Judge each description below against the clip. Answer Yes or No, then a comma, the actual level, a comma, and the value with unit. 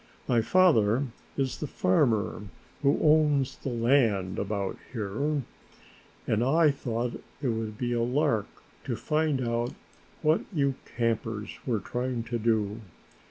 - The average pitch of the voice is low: Yes, low, 120 Hz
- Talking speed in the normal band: No, slow, 130 wpm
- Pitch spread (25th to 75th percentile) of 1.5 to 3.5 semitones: No, average, 4.0 semitones